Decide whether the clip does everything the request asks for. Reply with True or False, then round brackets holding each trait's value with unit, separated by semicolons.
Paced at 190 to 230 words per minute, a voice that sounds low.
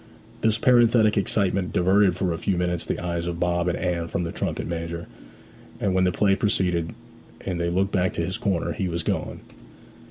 True (195 wpm; 90 Hz)